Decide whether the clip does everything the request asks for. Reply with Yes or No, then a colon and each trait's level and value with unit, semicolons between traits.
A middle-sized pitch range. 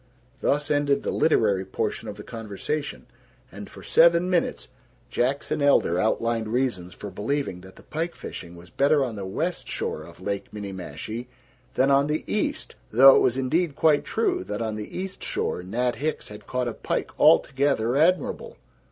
No: wide, 6.0 semitones